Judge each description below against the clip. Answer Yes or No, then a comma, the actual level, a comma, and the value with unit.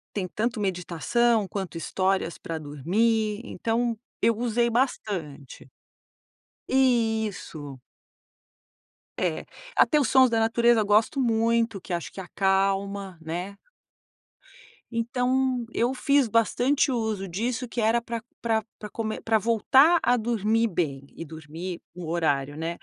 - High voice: Yes, high, 220 Hz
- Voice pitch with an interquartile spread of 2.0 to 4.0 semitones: No, average, 4.6 semitones